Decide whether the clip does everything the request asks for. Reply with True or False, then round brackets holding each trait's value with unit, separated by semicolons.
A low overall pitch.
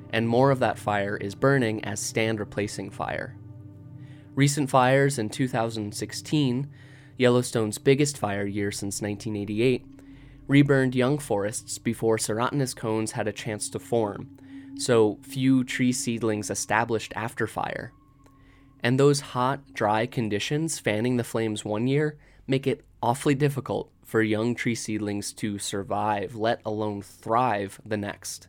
True (115 Hz)